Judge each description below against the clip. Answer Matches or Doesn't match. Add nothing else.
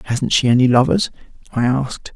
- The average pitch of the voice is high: Doesn't match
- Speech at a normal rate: Matches